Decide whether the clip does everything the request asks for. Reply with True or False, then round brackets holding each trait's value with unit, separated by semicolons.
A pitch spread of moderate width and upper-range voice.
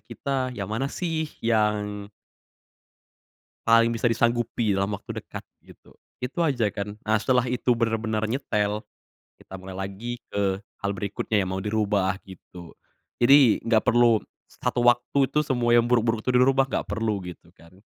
False (3.1 semitones; 115 Hz)